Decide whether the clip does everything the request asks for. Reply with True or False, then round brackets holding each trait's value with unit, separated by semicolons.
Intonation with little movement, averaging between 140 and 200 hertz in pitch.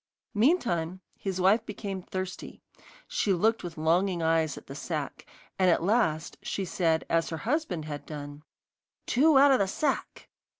False (5.1 semitones; 185 Hz)